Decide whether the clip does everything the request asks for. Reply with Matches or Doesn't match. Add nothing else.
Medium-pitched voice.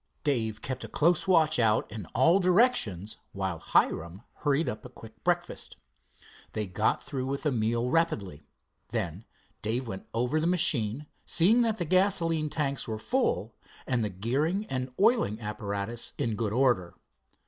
Doesn't match